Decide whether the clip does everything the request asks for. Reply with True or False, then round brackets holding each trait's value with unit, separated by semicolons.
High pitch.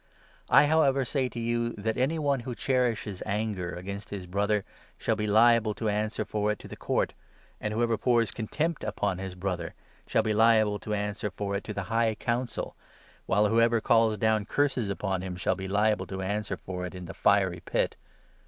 False (105 Hz)